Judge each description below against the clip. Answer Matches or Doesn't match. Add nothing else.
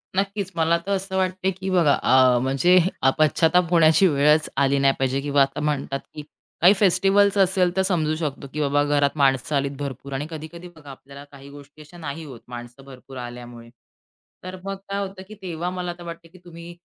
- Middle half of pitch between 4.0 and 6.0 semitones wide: Matches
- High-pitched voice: Doesn't match